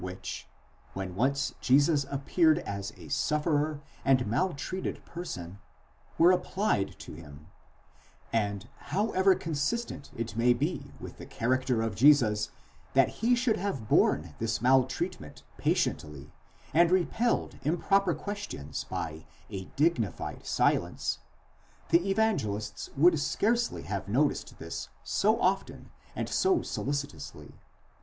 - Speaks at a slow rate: Yes, slow, 115 wpm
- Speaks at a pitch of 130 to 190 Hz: Yes, medium, 140 Hz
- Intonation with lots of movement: Yes, wide, 9.0 semitones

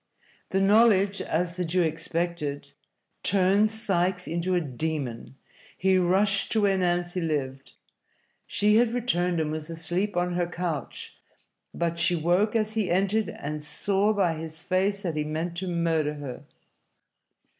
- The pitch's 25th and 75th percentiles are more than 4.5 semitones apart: No, average, 3.3 semitones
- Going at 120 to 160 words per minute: Yes, average, 145 wpm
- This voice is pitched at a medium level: Yes, medium, 175 Hz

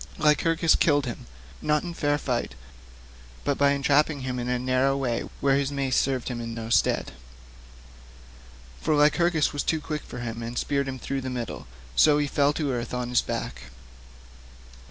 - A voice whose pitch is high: No, medium, 140 Hz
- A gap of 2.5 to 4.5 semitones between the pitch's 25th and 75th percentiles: Yes, average, 3.0 semitones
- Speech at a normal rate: Yes, average, 175 wpm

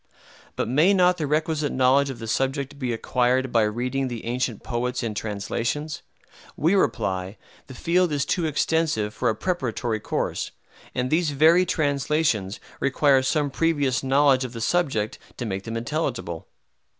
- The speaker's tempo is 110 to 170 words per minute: Yes, average, 155 wpm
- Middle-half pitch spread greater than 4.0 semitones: Yes, average, 4.6 semitones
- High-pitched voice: No, low, 130 Hz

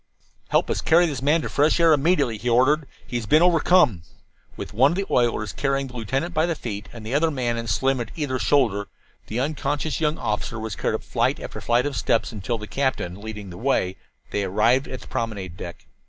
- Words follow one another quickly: Yes, fast, 220 wpm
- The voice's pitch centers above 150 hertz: No, low, 125 Hz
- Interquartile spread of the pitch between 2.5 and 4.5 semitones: No, average, 5.1 semitones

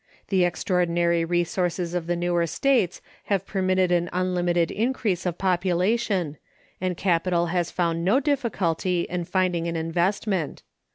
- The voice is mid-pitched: Yes, medium, 180 Hz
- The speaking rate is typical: No, slow, 130 wpm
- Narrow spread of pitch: Yes, narrow, 1.7 semitones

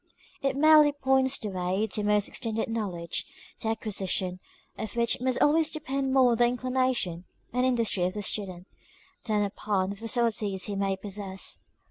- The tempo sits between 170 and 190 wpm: No, average, 160 wpm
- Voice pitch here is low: No, high, 220 Hz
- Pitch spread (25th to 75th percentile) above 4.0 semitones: Yes, average, 4.7 semitones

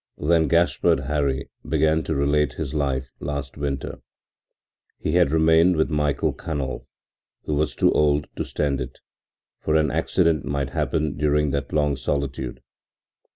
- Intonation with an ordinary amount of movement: No, narrow, 1.9 semitones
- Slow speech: No, average, 150 wpm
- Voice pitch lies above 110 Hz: No, very low, 75 Hz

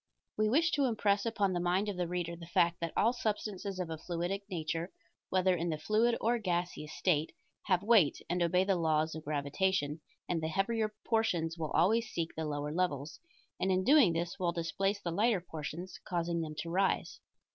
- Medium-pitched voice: Yes, medium, 180 Hz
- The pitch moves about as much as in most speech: Yes, average, 3.6 semitones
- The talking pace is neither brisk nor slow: Yes, average, 195 wpm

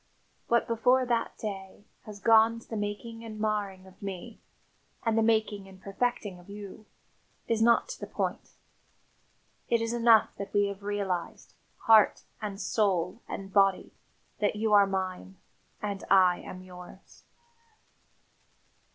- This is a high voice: Yes, high, 205 Hz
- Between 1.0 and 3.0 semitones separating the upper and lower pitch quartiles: Yes, average, 2.7 semitones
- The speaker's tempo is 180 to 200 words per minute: No, average, 145 wpm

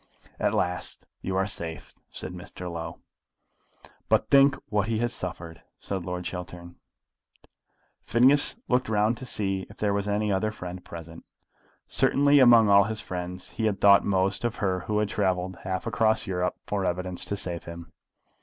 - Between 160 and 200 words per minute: Yes, average, 165 wpm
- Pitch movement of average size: Yes, average, 3.2 semitones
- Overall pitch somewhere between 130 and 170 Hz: No, very low, 95 Hz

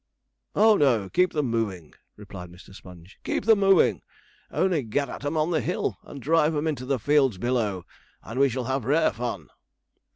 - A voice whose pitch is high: No, low, 130 Hz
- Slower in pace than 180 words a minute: No, average, 185 wpm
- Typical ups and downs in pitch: No, wide, 6.5 semitones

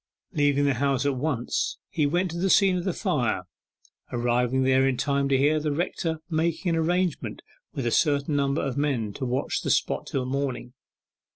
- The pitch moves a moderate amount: Yes, average, 3.5 semitones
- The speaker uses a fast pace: No, average, 190 wpm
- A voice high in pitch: No, medium, 140 Hz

